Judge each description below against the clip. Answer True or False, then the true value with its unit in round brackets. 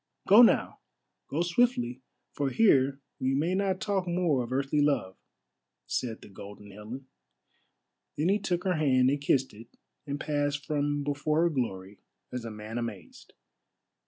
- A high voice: False (140 Hz)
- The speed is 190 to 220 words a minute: False (155 wpm)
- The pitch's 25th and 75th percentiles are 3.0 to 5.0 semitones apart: False (5.4 semitones)